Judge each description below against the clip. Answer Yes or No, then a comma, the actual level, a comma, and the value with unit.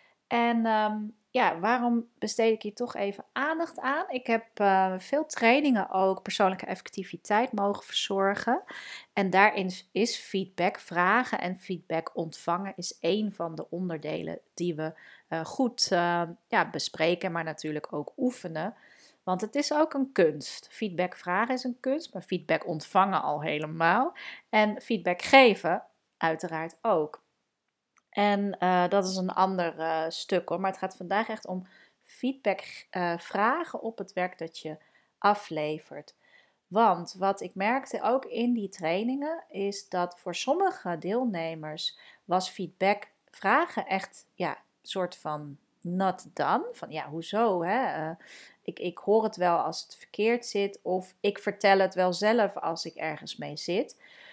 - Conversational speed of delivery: Yes, average, 150 wpm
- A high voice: Yes, high, 195 Hz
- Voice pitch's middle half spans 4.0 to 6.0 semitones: Yes, average, 4.3 semitones